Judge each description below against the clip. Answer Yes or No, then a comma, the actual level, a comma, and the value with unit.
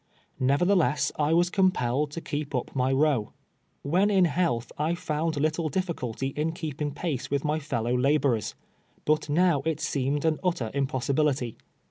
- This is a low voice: No, medium, 150 Hz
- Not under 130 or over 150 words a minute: No, average, 160 wpm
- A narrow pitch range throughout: No, average, 3.4 semitones